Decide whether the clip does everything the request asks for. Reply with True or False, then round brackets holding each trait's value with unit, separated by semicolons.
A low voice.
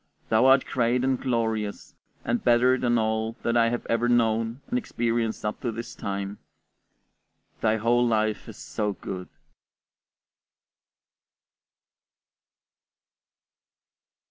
True (115 Hz)